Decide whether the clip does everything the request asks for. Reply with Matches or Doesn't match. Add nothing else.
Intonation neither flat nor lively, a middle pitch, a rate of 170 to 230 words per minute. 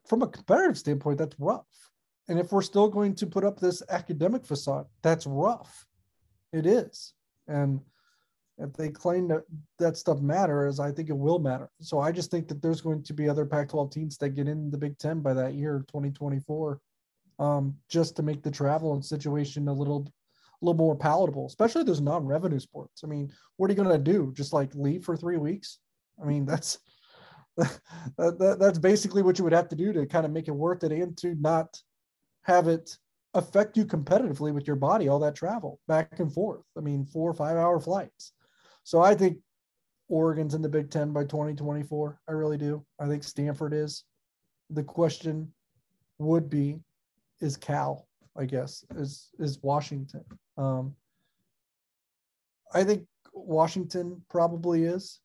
Matches